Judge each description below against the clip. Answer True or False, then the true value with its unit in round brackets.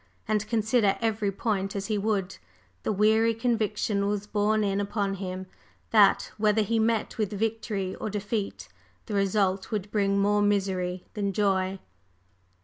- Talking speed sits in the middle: True (145 wpm)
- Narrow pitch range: True (1.7 semitones)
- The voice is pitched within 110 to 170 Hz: False (205 Hz)